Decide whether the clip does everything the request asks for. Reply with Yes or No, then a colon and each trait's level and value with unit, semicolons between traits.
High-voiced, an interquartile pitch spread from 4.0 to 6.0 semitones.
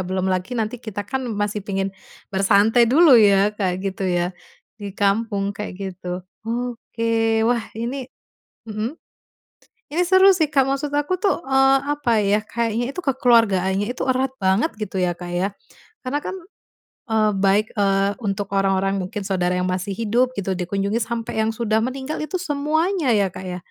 Yes: high, 215 Hz; average, 4.9 semitones